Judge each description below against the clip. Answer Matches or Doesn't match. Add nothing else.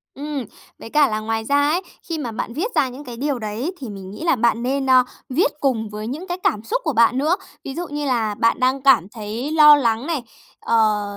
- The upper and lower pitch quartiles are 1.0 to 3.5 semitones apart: Doesn't match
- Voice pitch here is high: Matches